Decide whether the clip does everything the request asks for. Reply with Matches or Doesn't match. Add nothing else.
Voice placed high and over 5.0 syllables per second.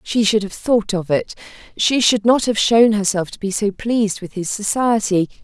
Doesn't match